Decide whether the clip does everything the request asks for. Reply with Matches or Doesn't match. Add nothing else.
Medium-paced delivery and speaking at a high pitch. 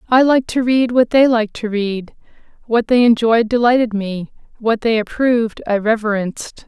Matches